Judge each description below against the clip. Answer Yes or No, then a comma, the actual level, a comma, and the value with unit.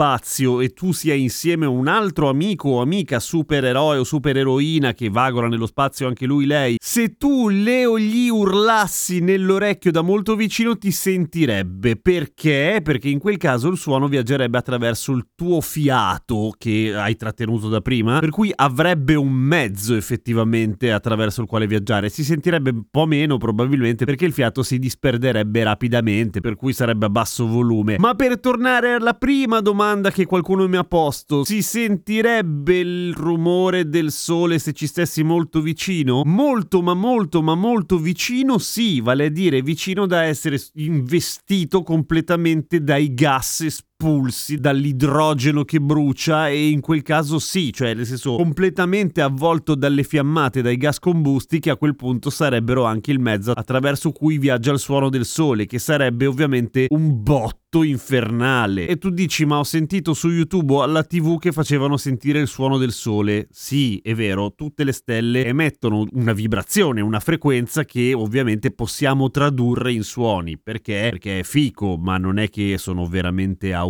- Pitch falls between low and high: Yes, medium, 145 Hz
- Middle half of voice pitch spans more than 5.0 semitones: Yes, wide, 5.6 semitones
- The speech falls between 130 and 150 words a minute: No, average, 165 wpm